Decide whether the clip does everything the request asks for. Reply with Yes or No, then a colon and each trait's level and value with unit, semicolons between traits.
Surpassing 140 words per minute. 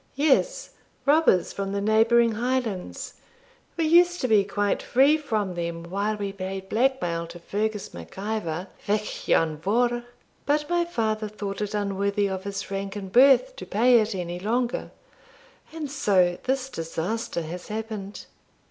Yes: average, 150 wpm